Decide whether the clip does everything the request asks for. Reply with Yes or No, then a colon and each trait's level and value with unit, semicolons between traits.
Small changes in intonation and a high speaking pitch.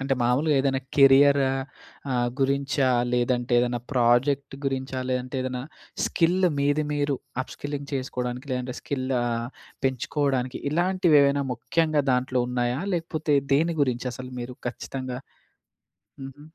No: narrow, 2.3 semitones; low, 135 Hz